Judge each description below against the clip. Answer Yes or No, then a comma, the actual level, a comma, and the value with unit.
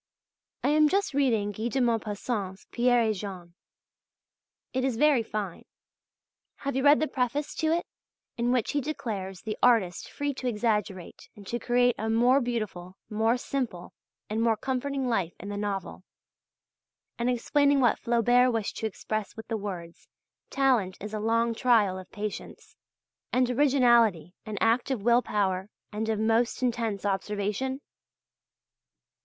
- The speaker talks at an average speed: Yes, average, 150 wpm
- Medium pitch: No, high, 230 Hz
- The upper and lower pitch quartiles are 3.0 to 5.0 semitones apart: Yes, average, 3.5 semitones